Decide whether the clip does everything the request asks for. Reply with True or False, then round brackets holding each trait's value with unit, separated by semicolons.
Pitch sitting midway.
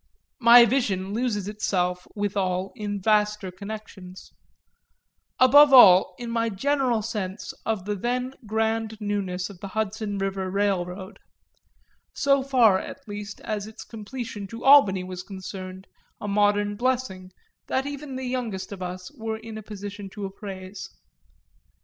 False (205 Hz)